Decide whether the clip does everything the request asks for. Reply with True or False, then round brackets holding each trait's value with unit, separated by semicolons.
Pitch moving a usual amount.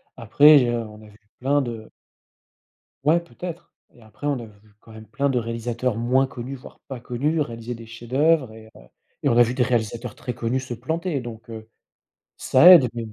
True (3.1 semitones)